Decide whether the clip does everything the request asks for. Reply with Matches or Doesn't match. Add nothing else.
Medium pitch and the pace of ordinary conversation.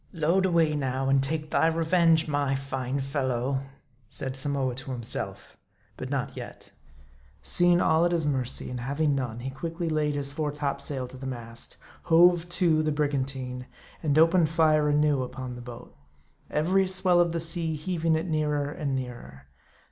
Matches